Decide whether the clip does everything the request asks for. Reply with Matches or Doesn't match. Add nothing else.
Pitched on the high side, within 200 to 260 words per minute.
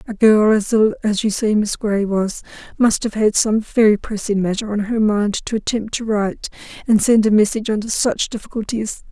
Matches